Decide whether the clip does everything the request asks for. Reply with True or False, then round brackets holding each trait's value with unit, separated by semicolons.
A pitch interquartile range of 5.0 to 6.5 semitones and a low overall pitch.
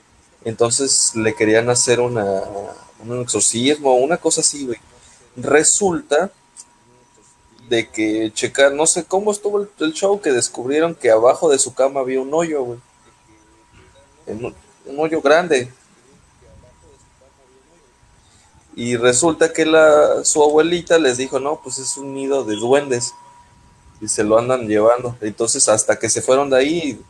True (5.3 semitones; 130 Hz)